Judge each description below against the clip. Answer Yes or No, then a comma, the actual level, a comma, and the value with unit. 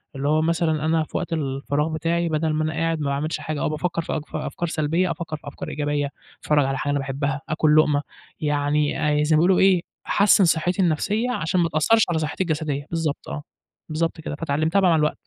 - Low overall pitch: No, medium, 155 Hz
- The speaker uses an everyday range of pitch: No, narrow, 2.1 semitones